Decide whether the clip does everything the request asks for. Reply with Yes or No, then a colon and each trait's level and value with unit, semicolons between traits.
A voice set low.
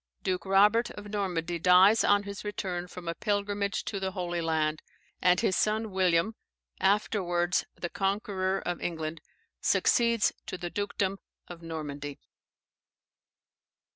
No: medium, 185 Hz